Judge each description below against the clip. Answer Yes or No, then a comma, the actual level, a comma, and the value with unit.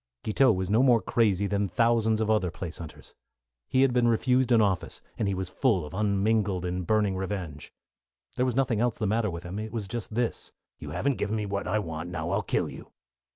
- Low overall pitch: Yes, low, 105 Hz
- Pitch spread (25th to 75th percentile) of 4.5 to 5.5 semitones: No, average, 3.7 semitones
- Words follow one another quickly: Yes, fast, 220 wpm